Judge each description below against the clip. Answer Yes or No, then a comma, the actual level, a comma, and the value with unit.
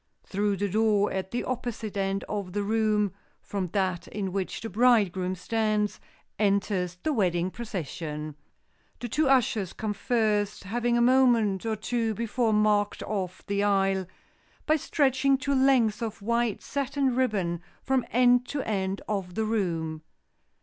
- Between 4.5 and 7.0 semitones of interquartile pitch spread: No, average, 3.7 semitones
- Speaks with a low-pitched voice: No, high, 210 Hz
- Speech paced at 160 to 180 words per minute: No, average, 150 wpm